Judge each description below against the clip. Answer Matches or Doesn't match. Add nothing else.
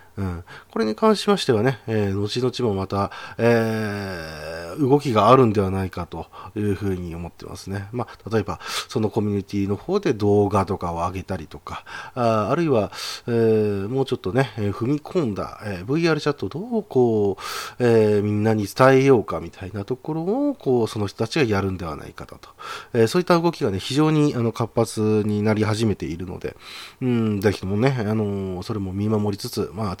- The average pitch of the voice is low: Matches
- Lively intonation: Doesn't match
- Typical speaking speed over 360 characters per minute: Matches